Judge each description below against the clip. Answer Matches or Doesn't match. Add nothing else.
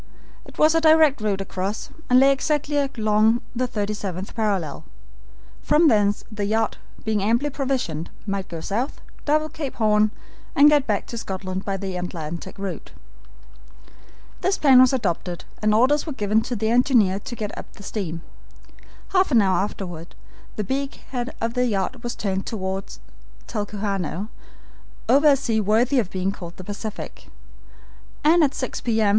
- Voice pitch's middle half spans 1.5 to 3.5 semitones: Doesn't match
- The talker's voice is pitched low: Doesn't match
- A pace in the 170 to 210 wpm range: Doesn't match